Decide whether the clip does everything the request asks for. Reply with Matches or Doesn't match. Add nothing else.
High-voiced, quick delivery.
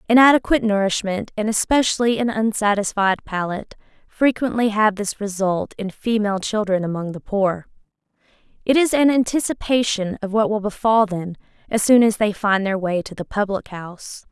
Doesn't match